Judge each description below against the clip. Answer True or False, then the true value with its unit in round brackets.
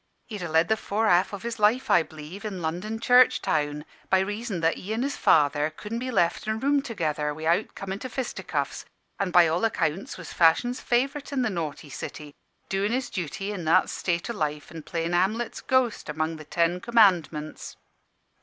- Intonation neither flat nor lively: False (5.8 semitones)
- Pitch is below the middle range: False (185 Hz)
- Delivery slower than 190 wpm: False (195 wpm)